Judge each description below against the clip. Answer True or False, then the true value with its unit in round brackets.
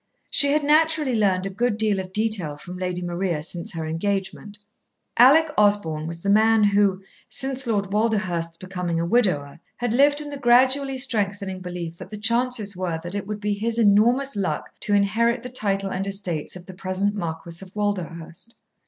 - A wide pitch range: False (4.4 semitones)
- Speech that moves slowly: False (180 wpm)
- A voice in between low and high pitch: False (200 Hz)